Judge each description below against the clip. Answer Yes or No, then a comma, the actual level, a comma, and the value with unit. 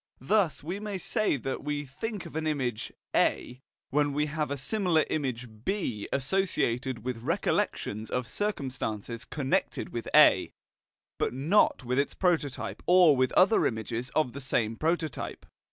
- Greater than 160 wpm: No, average, 150 wpm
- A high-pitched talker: No, medium, 140 Hz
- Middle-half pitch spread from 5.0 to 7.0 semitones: Yes, average, 5.3 semitones